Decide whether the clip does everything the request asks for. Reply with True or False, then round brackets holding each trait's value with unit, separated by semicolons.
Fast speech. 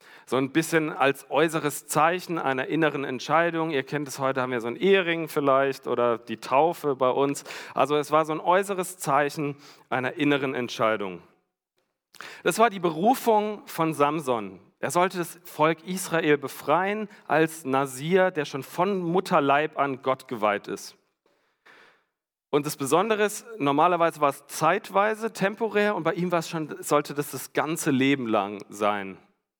False (160 wpm)